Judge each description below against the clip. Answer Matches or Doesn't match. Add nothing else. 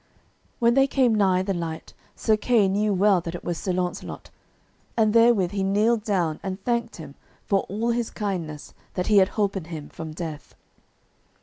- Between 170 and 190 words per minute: Matches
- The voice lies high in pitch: Matches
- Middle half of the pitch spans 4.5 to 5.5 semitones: Doesn't match